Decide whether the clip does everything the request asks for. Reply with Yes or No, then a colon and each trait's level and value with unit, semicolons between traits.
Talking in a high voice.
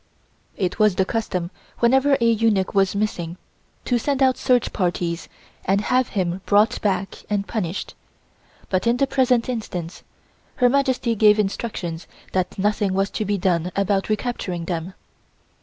Yes: high, 205 Hz